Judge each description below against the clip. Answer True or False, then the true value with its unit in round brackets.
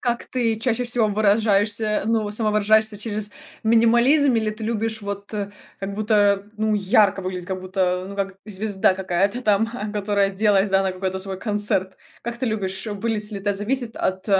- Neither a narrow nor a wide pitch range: False (2.1 semitones)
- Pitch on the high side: True (210 Hz)